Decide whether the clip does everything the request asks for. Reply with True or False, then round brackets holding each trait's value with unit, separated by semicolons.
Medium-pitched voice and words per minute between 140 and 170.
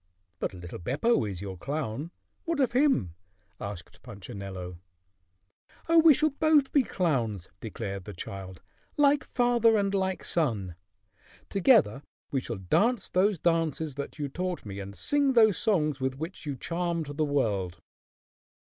True (150 Hz; 145 wpm)